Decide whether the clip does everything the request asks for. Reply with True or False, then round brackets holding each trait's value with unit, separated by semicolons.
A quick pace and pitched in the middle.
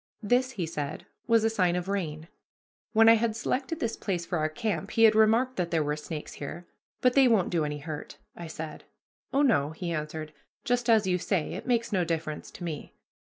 True (215 wpm; 180 Hz)